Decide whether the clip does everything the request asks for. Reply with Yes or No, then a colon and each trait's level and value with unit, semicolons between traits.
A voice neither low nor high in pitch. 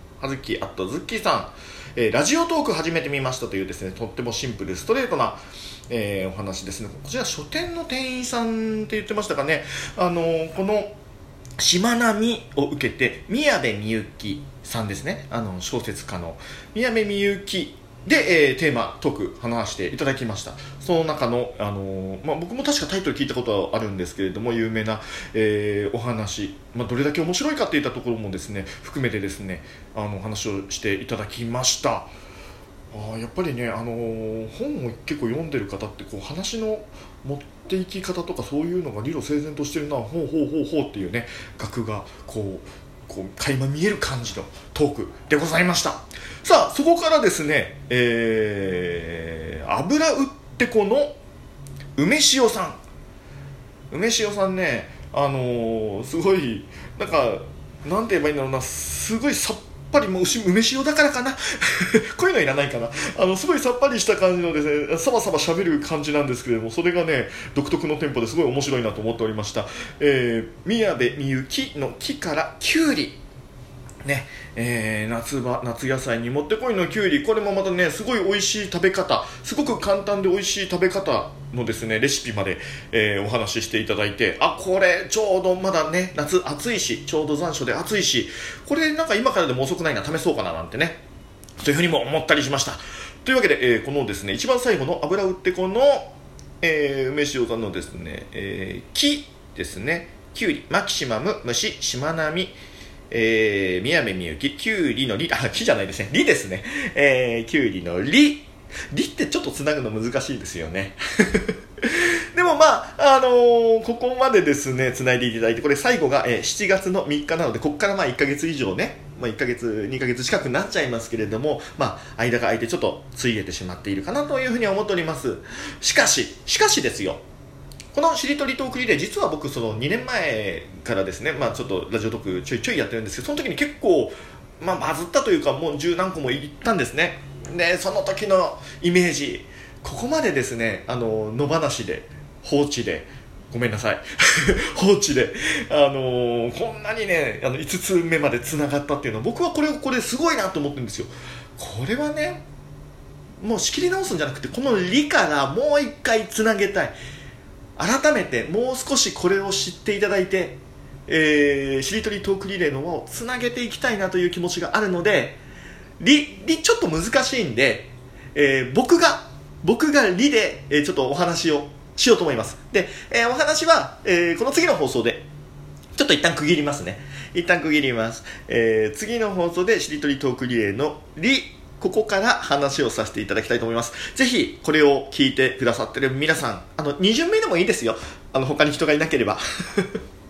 Yes: medium, 145 Hz